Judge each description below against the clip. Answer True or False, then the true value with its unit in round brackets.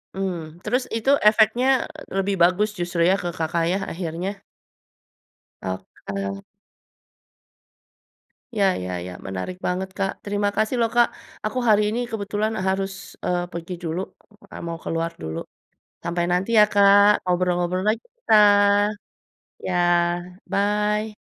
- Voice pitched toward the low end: False (190 Hz)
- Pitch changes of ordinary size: True (3.6 semitones)